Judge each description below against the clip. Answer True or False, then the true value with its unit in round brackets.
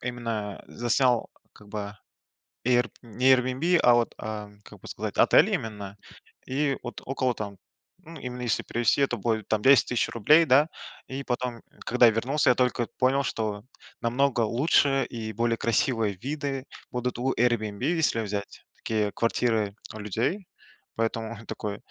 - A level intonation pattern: False (3.1 semitones)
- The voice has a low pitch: True (120 Hz)